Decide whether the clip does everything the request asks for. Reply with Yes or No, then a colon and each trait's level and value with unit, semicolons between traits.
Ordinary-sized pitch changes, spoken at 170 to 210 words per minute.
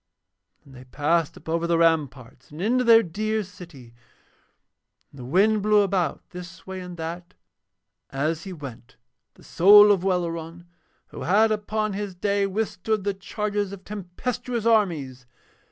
No: average, 4.2 semitones; average, 150 wpm